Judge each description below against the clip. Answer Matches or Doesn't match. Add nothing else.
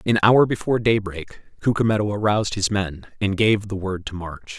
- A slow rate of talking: Doesn't match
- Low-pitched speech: Matches